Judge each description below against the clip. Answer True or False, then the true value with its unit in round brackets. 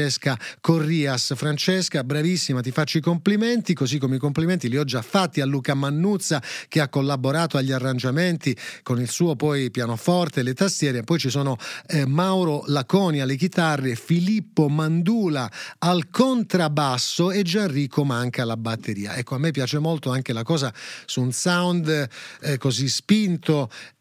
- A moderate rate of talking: True (155 wpm)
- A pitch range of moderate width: True (4.5 semitones)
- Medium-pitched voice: True (150 Hz)